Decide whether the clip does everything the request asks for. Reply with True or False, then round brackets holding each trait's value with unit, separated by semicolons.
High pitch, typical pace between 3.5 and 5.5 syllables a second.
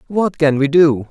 False (155 Hz; 4.4 syllables/s)